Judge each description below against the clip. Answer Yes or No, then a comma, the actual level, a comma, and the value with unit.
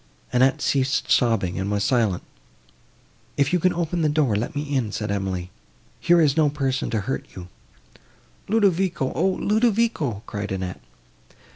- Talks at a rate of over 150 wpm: No, average, 145 wpm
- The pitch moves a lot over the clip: Yes, wide, 8.3 semitones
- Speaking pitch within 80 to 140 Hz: Yes, low, 135 Hz